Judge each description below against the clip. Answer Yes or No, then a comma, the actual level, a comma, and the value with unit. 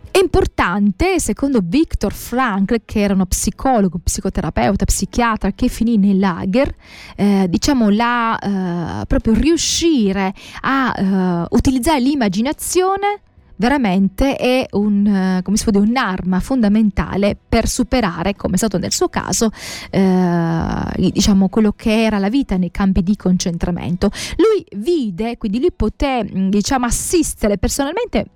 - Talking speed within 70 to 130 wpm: Yes, average, 125 wpm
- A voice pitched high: Yes, high, 215 Hz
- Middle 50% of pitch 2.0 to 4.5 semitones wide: No, average, 5.2 semitones